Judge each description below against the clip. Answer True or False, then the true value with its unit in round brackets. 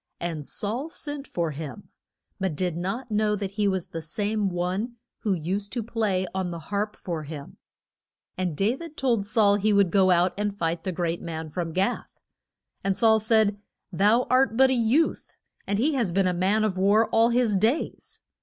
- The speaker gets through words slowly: False (190 wpm)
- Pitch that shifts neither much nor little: True (3.9 semitones)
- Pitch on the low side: False (200 Hz)